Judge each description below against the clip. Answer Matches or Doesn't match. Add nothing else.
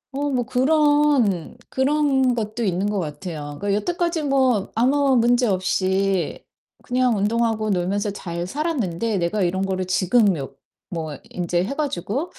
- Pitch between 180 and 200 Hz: Doesn't match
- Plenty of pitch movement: Matches